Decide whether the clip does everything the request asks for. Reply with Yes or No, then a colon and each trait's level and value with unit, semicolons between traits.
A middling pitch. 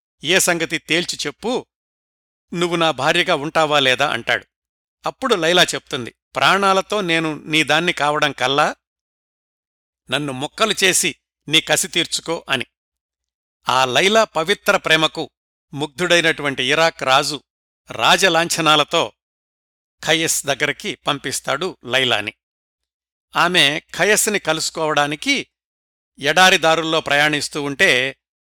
Yes: medium, 150 Hz